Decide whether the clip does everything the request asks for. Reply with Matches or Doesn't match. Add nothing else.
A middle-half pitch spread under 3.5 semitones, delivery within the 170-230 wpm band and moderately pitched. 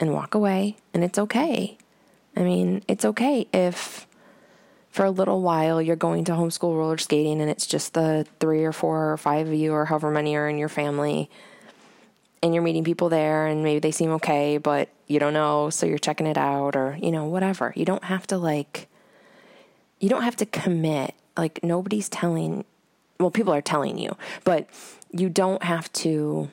Matches